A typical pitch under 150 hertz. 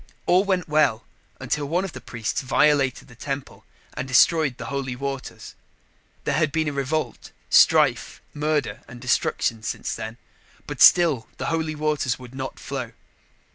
Yes: medium, 140 Hz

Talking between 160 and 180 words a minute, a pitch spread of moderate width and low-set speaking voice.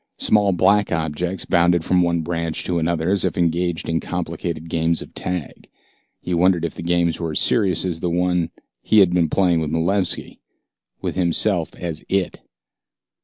No: average, 170 wpm; narrow, 1.6 semitones; very low, 85 Hz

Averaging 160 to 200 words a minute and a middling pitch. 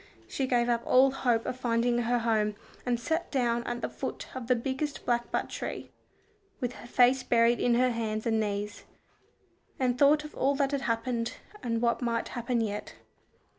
No: average, 180 wpm; high, 240 Hz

